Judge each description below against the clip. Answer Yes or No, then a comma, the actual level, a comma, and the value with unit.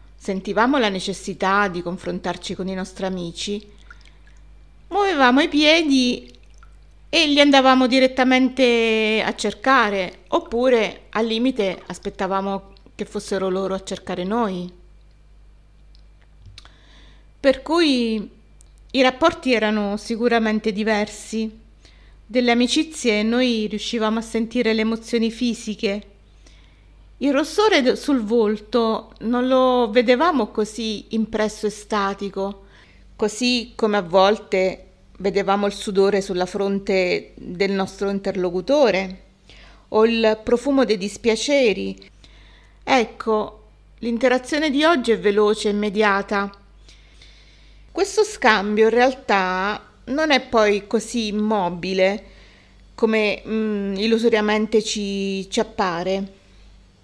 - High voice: Yes, high, 215 Hz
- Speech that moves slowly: Yes, slow, 100 wpm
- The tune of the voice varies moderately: Yes, average, 3.7 semitones